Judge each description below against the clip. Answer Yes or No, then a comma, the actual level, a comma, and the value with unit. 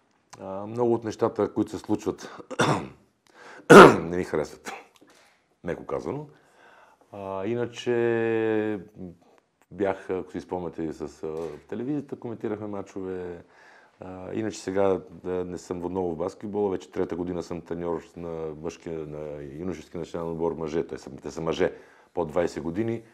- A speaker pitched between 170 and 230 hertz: No, very low, 90 Hz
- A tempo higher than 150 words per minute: No, average, 130 wpm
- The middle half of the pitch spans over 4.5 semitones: No, average, 4.2 semitones